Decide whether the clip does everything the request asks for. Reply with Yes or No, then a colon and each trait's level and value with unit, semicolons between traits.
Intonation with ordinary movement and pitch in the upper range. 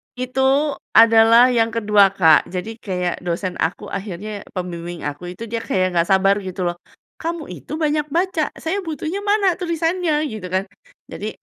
No: wide, 8.8 semitones; high, 225 Hz